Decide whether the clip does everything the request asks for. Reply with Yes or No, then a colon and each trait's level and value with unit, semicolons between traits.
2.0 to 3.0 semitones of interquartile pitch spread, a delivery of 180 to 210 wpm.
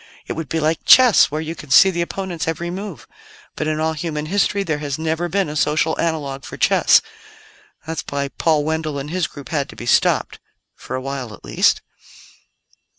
Yes: narrow, 2.5 semitones; average, 200 wpm